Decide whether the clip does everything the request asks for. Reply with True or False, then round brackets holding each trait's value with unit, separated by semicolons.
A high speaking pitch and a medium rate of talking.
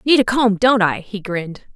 False (210 Hz; 240 wpm)